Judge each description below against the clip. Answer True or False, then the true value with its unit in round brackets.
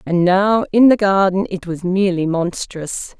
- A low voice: False (185 Hz)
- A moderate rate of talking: True (170 wpm)